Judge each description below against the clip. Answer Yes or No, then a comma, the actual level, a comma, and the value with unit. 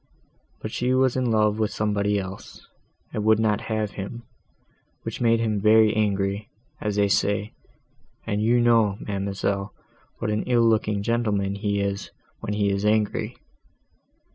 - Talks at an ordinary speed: Yes, average, 150 wpm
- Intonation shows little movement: Yes, narrow, 1.7 semitones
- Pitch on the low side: Yes, low, 105 Hz